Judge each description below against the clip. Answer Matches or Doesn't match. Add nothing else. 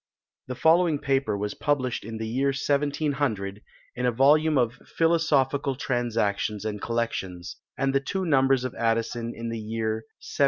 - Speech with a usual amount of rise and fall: Matches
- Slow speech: Doesn't match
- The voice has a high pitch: Doesn't match